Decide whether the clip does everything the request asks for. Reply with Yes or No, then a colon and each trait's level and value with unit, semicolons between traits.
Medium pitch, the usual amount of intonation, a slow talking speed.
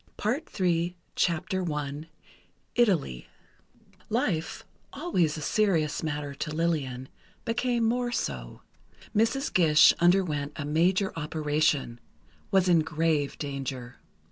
Yes: medium, 160 Hz; average, 4.3 semitones; slow, 95 wpm